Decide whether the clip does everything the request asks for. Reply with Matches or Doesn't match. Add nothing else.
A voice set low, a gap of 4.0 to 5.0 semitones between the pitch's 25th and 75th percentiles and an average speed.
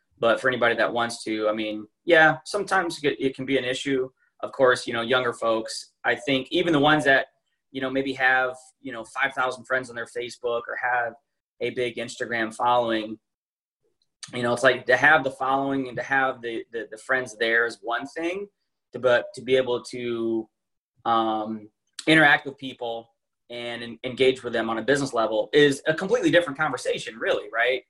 Doesn't match